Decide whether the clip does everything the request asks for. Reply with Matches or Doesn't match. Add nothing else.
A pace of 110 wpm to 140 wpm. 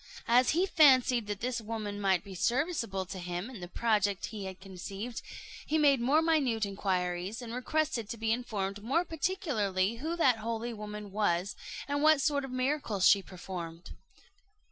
Doesn't match